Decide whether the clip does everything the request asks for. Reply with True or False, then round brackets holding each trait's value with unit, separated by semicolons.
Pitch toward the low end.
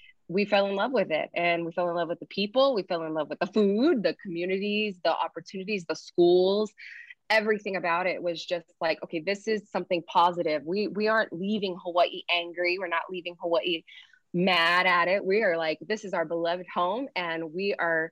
False (180 Hz)